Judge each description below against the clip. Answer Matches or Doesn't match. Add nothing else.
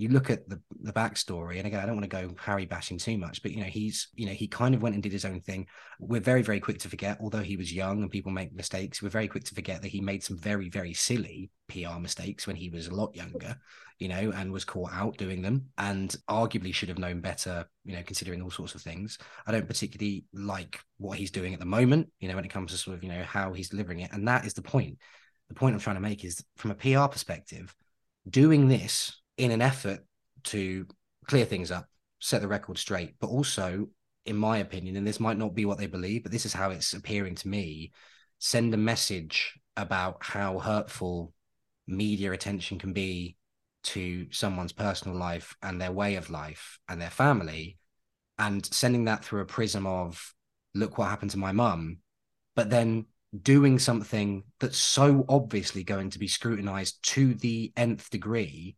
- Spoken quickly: Matches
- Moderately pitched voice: Doesn't match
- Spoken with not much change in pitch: Doesn't match